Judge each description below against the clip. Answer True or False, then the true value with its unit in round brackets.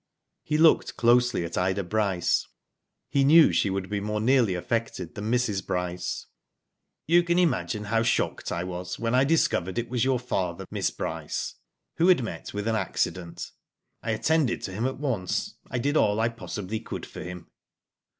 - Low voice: True (110 Hz)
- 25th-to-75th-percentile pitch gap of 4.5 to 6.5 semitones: True (5.3 semitones)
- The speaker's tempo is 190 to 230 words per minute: False (175 wpm)